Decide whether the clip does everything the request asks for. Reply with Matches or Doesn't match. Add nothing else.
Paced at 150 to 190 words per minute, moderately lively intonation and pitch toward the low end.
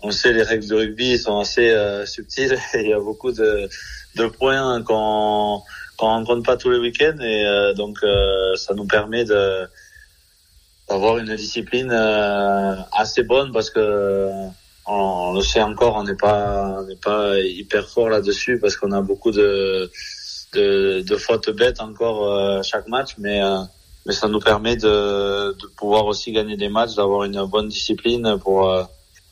Matches